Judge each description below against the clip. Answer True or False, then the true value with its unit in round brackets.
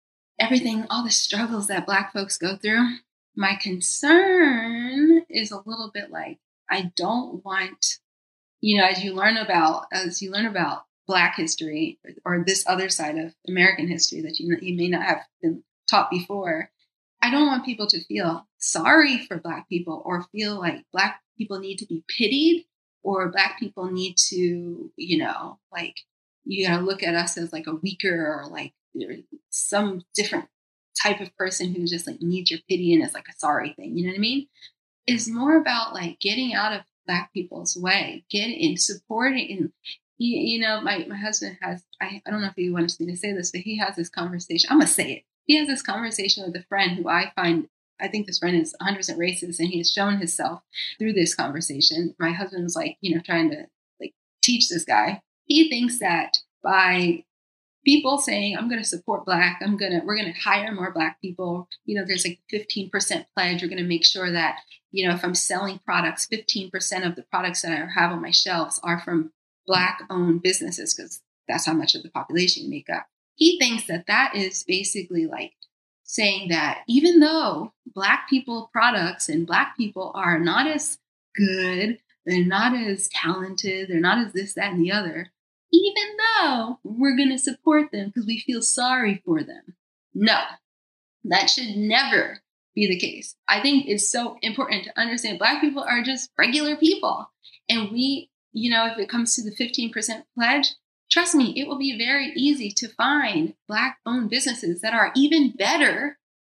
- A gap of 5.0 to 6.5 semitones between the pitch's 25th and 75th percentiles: True (5.5 semitones)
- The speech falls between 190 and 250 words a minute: True (195 wpm)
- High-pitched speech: True (200 Hz)